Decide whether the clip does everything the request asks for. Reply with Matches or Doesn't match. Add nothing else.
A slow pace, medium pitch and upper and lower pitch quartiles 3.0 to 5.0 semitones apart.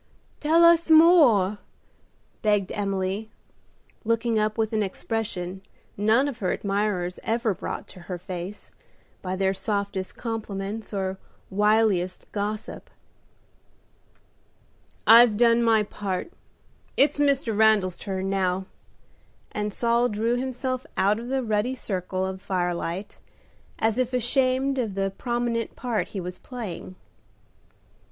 Doesn't match